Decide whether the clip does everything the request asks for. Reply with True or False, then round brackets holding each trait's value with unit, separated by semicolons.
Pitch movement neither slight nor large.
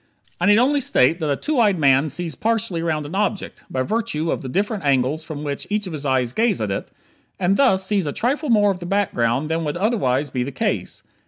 False (6.7 semitones)